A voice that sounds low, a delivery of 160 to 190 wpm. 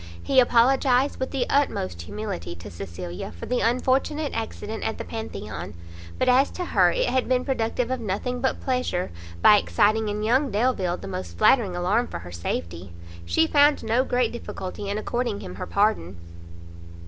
No: high, 220 Hz; average, 170 wpm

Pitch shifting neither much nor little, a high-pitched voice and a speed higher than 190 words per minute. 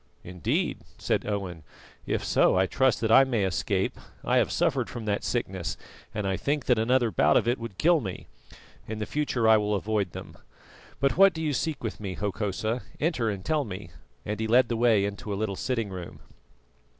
No: average, 4.0 semitones; low, 110 Hz; average, 200 wpm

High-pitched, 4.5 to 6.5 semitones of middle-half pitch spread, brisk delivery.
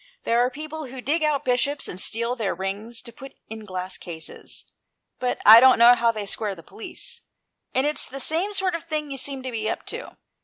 Yes: very high, 250 Hz; average, 5.2 semitones; fast, 220 wpm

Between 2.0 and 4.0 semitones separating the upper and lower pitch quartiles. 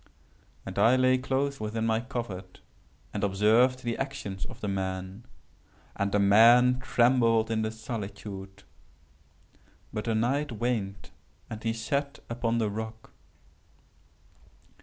Yes: average, 3.6 semitones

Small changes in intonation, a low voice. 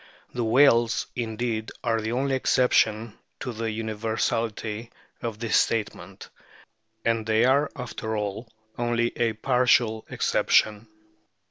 Yes: narrow, 1.6 semitones; low, 115 Hz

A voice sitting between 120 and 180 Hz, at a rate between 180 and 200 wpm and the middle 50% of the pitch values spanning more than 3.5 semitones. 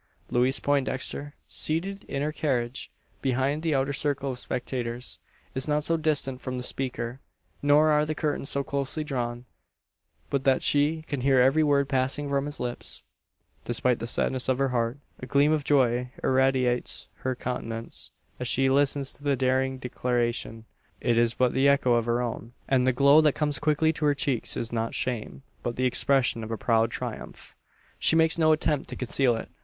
No: low, 135 Hz; average, 185 wpm; average, 2.7 semitones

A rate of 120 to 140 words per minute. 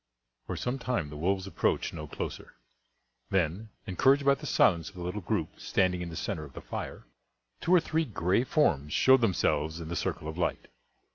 No: average, 195 wpm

